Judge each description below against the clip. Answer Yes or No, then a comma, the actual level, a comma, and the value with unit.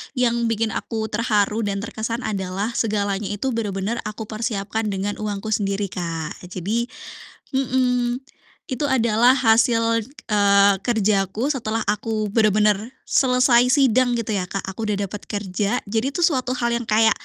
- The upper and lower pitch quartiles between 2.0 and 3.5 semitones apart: Yes, average, 2.7 semitones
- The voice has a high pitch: Yes, high, 220 Hz